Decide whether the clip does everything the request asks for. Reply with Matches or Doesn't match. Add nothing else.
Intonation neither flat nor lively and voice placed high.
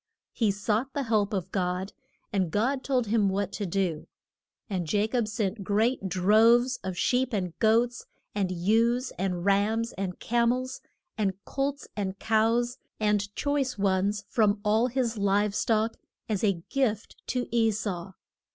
Matches